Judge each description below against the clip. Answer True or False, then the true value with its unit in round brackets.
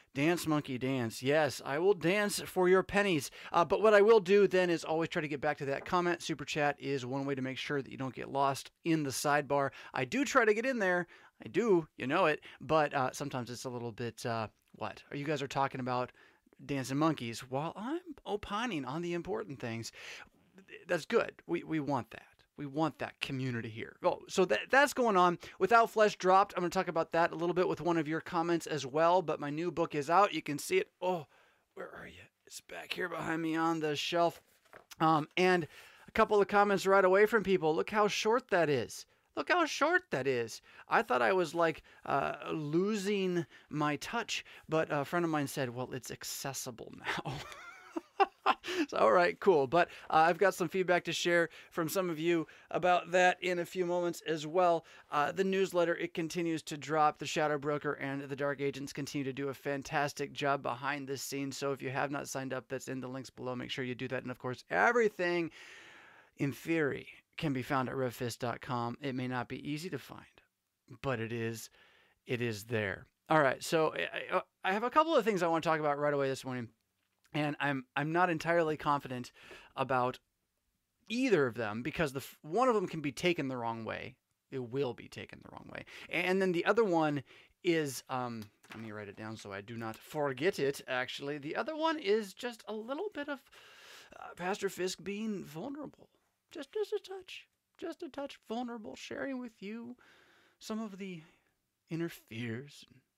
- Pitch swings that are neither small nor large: False (5.8 semitones)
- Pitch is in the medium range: True (160 Hz)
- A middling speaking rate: False (210 wpm)